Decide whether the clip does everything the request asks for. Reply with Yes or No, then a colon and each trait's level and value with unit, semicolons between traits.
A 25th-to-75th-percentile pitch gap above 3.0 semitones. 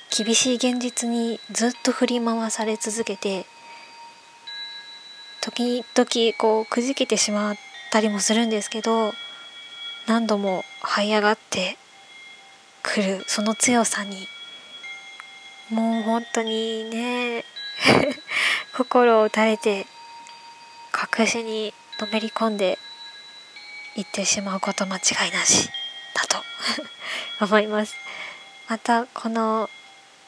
No: narrow, 2.3 semitones